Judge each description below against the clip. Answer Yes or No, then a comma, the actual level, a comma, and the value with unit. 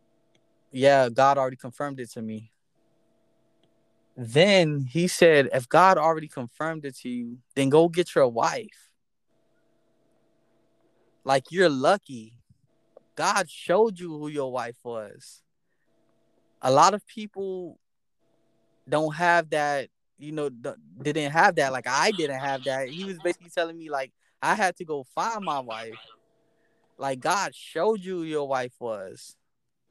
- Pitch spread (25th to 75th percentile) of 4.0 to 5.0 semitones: Yes, average, 4.7 semitones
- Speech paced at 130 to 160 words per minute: Yes, average, 140 wpm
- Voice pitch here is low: No, medium, 145 Hz